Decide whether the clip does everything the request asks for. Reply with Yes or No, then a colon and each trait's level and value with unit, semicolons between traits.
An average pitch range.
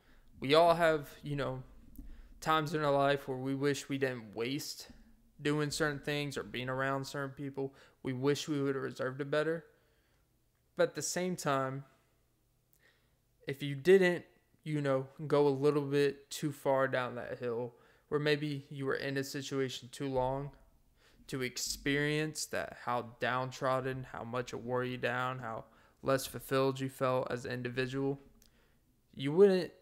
No: narrow, 2.2 semitones